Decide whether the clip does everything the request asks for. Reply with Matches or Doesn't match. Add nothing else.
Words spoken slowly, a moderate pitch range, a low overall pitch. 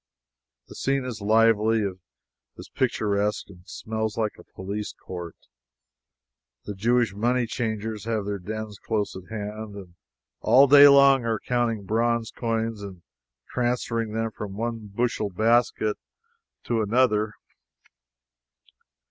Doesn't match